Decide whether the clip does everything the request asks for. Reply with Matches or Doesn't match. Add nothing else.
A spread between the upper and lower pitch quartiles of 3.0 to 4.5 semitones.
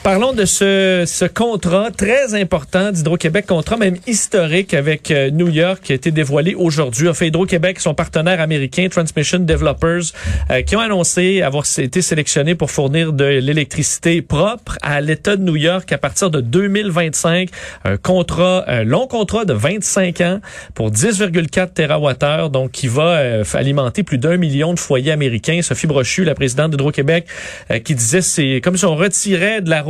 Matches